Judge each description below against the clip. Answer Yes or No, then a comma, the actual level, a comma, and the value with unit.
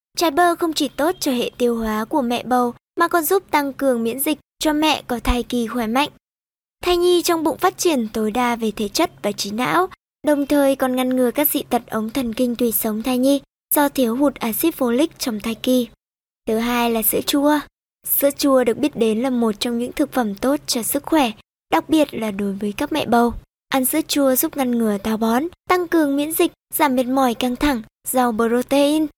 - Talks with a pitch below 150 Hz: No, very high, 260 Hz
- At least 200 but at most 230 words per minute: Yes, average, 225 wpm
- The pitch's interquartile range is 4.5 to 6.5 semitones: No, average, 4.0 semitones